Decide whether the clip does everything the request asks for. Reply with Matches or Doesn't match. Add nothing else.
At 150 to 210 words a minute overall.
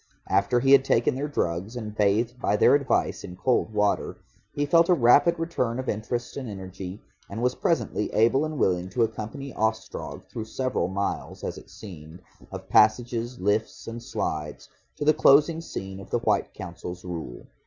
Matches